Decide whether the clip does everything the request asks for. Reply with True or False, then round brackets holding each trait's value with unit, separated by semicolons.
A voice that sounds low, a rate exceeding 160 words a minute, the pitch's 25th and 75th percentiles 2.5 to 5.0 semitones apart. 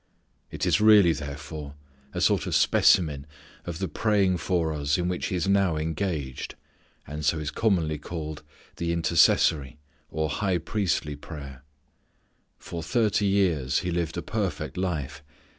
False (85 Hz; 145 wpm; 3.6 semitones)